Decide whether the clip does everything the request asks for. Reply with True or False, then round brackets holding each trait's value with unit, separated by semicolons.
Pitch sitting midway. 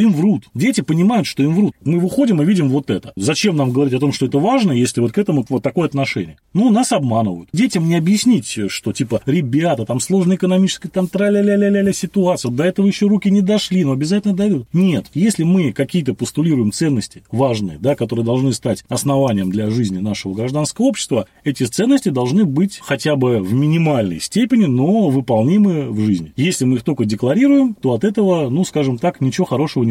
True (150 Hz)